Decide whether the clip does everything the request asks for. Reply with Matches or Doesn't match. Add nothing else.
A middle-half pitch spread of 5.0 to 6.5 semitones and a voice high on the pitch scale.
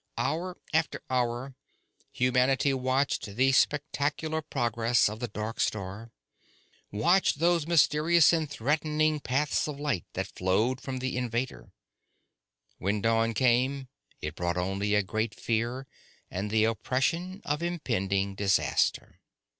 Doesn't match